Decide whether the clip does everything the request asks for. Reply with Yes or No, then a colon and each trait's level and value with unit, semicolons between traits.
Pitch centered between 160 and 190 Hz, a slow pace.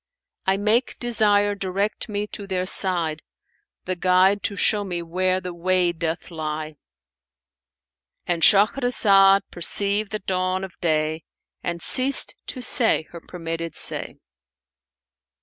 Yes: medium, 185 Hz; slow, 130 wpm